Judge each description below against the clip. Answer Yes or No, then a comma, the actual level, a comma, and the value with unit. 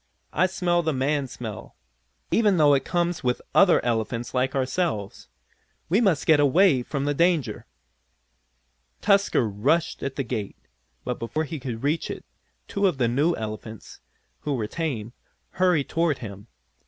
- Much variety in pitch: Yes, wide, 6.0 semitones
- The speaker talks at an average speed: Yes, average, 155 wpm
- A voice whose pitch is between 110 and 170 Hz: Yes, medium, 140 Hz